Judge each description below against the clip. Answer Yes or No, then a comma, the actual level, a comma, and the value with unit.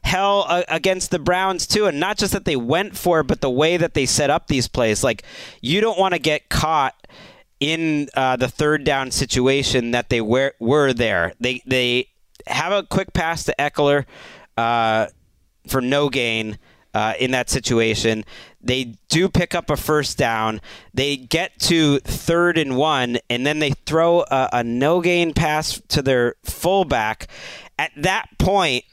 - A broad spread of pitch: No, average, 4.9 semitones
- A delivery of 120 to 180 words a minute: Yes, average, 175 wpm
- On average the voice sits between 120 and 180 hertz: Yes, medium, 140 Hz